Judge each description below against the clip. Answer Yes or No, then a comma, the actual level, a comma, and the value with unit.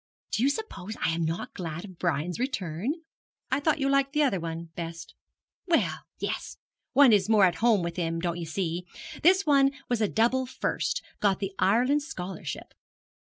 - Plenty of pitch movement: Yes, wide, 8.1 semitones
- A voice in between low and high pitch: No, high, 205 Hz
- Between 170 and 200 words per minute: Yes, average, 180 wpm